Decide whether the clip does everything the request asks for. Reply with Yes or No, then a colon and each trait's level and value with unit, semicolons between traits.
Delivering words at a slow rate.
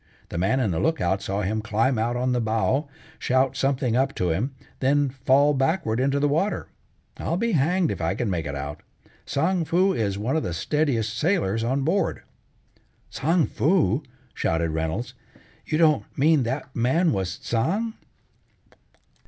No: average, 165 wpm